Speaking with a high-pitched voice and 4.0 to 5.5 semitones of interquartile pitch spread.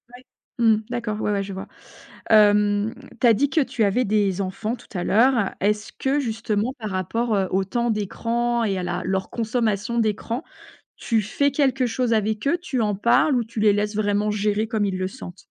No: high, 215 Hz; average, 2.7 semitones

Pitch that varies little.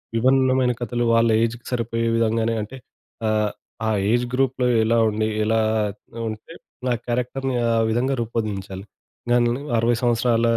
Yes: narrow, 1.7 semitones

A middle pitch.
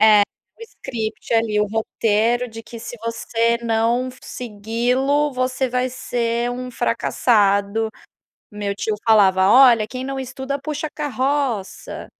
No: high, 235 Hz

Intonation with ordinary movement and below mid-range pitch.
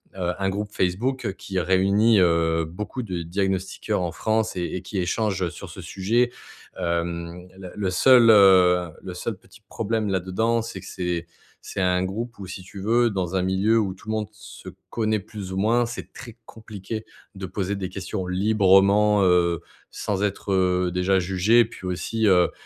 Yes: average, 3.0 semitones; very low, 95 Hz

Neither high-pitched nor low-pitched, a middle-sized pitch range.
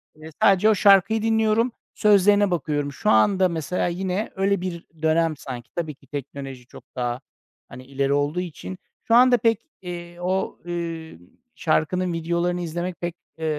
Yes: medium, 175 Hz; average, 4.1 semitones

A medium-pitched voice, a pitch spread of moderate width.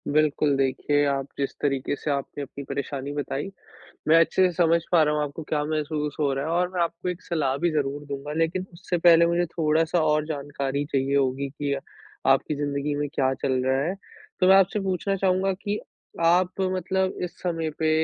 Yes: medium, 150 Hz; average, 3.6 semitones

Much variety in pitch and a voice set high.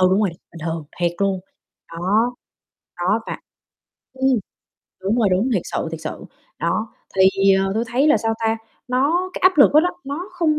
Yes: wide, 6.9 semitones; high, 220 Hz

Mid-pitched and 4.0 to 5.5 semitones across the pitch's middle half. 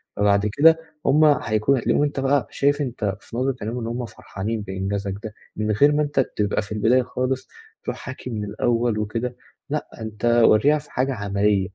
No: low, 115 Hz; average, 4.4 semitones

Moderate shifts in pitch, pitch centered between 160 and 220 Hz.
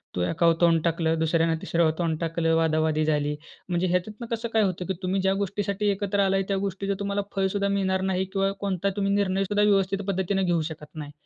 Yes: average, 3.2 semitones; high, 190 Hz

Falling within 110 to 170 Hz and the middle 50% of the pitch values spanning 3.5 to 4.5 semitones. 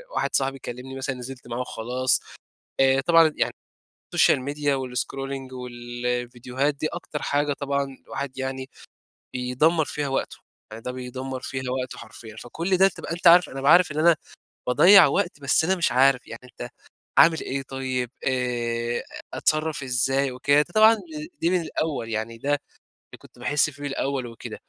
No: low, 135 Hz; average, 2.8 semitones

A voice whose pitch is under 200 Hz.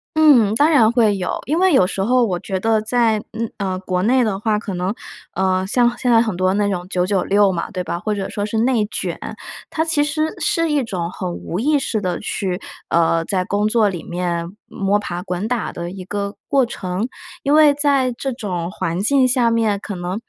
No: high, 205 Hz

